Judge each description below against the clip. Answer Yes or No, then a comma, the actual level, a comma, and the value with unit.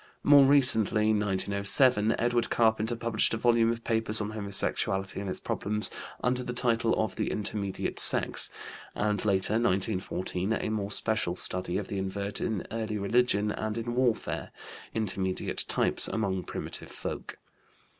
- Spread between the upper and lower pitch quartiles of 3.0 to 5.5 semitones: No, narrow, 2.5 semitones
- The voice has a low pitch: Yes, low, 110 Hz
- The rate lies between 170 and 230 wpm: No, average, 145 wpm